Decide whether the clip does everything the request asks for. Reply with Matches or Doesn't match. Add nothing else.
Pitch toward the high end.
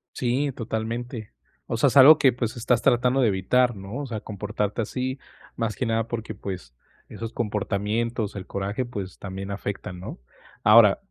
Doesn't match